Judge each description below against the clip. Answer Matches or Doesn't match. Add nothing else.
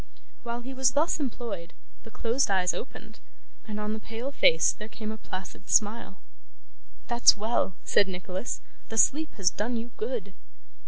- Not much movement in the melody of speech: Doesn't match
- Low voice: Doesn't match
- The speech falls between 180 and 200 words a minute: Doesn't match